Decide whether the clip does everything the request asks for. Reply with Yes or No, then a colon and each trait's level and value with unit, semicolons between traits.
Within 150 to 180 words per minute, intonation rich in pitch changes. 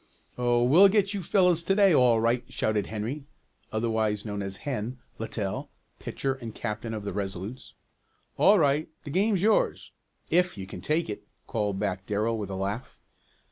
Yes: average, 170 wpm; wide, 6.9 semitones